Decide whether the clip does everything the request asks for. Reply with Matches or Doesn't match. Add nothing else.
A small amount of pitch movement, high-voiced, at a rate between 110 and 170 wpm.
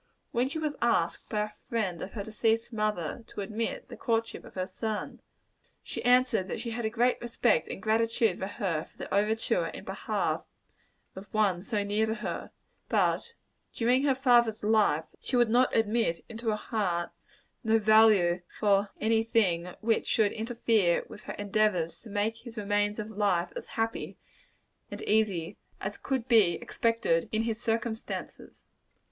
Matches